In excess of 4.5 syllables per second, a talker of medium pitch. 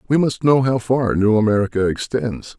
No: 5.0 syllables/s; low, 115 Hz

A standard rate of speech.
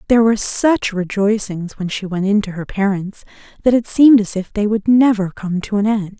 No: fast, 225 wpm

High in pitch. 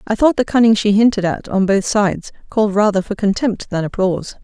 Yes: high, 210 Hz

